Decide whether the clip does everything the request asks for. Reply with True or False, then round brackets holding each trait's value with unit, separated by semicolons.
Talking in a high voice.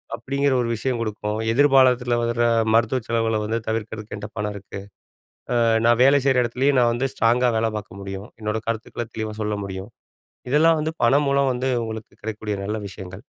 False (115 Hz)